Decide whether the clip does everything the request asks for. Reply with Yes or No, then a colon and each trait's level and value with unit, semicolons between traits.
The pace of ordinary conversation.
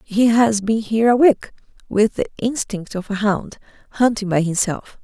Yes: average, 180 wpm